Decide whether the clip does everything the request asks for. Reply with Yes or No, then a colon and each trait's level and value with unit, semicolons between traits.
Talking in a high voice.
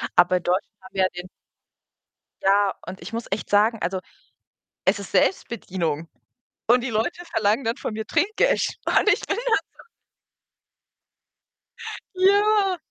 Yes: high, 220 Hz